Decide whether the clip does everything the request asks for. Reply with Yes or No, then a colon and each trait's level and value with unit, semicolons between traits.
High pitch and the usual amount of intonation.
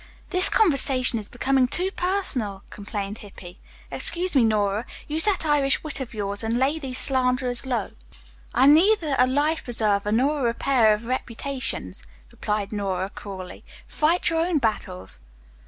No: very high, 250 Hz; wide, 6.0 semitones